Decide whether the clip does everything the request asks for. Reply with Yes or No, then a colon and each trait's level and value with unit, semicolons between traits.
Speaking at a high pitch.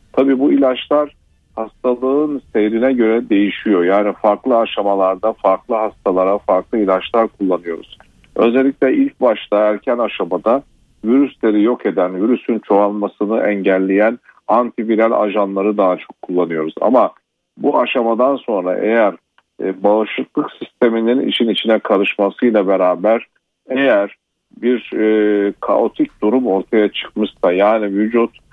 No: low, 110 Hz